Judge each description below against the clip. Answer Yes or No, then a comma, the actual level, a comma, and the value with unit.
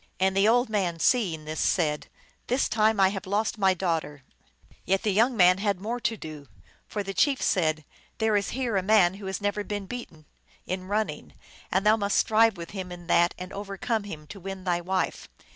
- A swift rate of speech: Yes, fast, 215 wpm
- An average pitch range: Yes, average, 3.3 semitones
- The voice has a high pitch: Yes, high, 195 Hz